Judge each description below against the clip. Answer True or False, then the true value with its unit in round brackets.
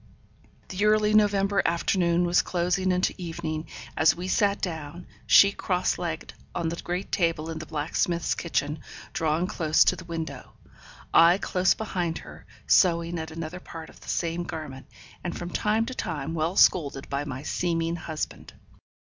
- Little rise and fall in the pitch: True (2.2 semitones)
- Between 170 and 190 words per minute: False (160 wpm)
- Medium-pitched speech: True (170 Hz)